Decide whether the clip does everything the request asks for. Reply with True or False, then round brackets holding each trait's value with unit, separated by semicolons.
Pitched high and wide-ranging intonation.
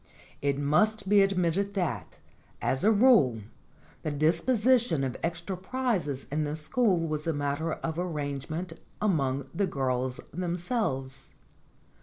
False (165 Hz; 5.9 semitones)